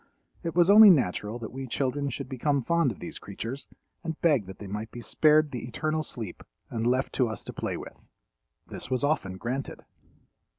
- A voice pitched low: Yes, low, 130 Hz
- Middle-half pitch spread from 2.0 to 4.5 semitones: No, average, 5.0 semitones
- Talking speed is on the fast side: No, average, 195 wpm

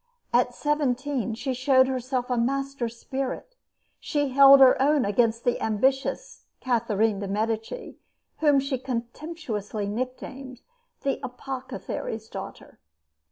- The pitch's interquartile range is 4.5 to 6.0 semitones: No, average, 2.9 semitones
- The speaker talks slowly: Yes, slow, 115 wpm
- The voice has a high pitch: Yes, very high, 255 Hz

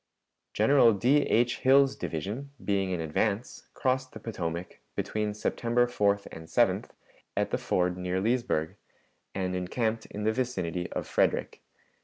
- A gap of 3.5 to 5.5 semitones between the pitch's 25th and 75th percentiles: Yes, average, 5.1 semitones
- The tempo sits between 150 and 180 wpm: No, average, 140 wpm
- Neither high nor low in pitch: No, low, 105 Hz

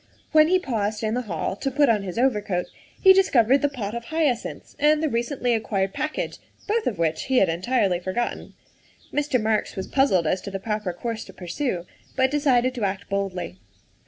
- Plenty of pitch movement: Yes, wide, 5.8 semitones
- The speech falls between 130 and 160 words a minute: No, average, 190 wpm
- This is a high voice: Yes, high, 230 Hz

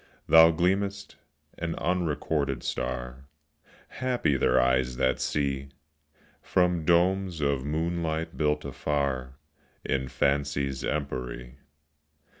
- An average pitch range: Yes, average, 4.2 semitones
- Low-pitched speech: Yes, very low, 75 Hz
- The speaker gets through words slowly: Yes, slow, 90 wpm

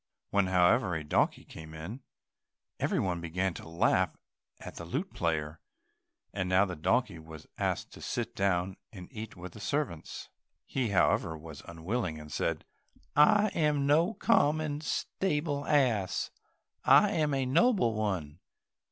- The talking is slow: No, average, 145 wpm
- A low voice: Yes, very low, 95 Hz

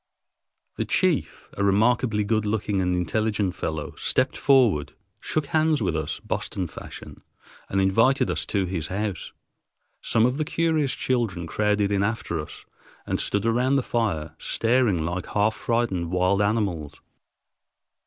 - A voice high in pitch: No, low, 105 Hz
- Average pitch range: Yes, average, 4.6 semitones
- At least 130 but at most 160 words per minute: Yes, average, 145 wpm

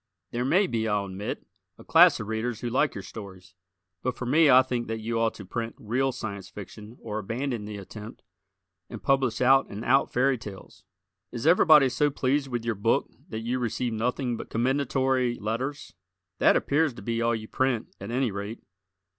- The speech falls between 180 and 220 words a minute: Yes, average, 190 wpm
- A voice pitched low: Yes, low, 120 Hz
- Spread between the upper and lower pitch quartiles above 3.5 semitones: No, average, 3.2 semitones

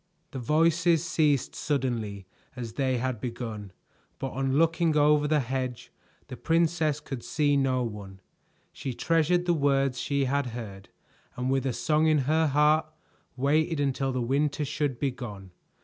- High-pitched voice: No, medium, 140 Hz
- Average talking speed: Yes, average, 155 wpm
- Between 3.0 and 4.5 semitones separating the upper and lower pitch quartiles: Yes, average, 3.5 semitones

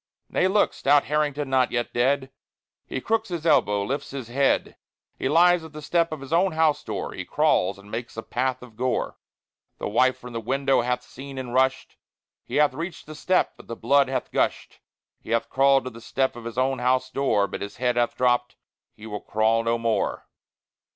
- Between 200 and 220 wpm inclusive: Yes, fast, 205 wpm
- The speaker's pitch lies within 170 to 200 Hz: No, low, 130 Hz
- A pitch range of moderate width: Yes, average, 3.3 semitones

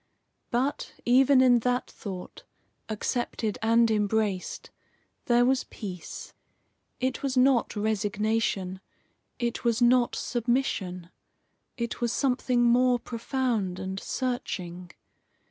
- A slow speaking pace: Yes, slow, 100 wpm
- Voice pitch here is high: Yes, high, 235 Hz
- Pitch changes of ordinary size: Yes, average, 3.3 semitones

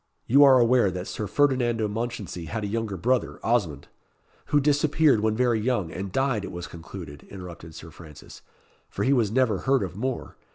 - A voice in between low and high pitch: No, low, 110 Hz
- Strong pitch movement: Yes, wide, 5.8 semitones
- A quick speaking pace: No, average, 190 wpm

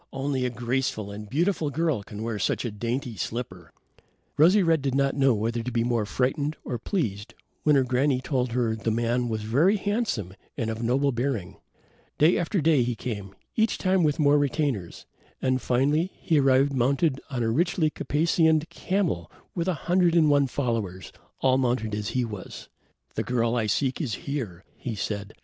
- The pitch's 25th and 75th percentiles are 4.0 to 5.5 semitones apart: Yes, average, 4.7 semitones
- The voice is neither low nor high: No, low, 130 Hz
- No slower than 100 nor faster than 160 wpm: No, average, 180 wpm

